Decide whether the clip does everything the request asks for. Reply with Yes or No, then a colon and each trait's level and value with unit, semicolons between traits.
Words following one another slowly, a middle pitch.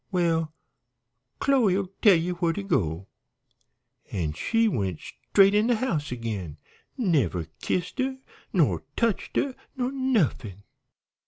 Yes: slow, 120 wpm; medium, 180 Hz